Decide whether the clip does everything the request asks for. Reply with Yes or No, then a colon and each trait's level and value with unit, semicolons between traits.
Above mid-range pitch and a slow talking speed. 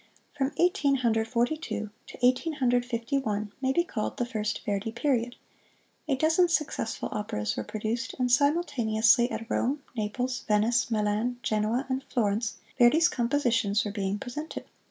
No: high, 240 Hz; average, 155 wpm